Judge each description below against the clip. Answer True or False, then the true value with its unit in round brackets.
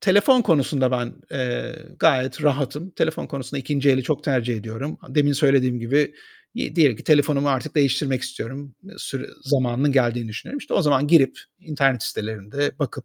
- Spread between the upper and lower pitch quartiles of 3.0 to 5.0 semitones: False (2.6 semitones)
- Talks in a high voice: False (140 Hz)